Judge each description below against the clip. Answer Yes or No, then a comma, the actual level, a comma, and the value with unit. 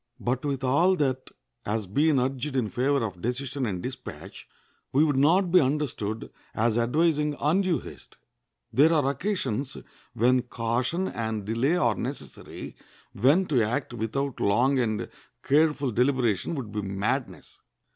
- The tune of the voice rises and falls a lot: No, average, 4.4 semitones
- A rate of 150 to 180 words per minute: No, average, 140 wpm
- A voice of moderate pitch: No, low, 130 Hz